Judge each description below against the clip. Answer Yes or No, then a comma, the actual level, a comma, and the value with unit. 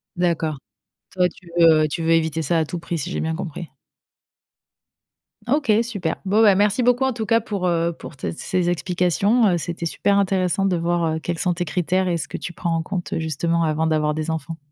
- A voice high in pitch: No, medium, 175 Hz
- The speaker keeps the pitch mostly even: No, average, 3.0 semitones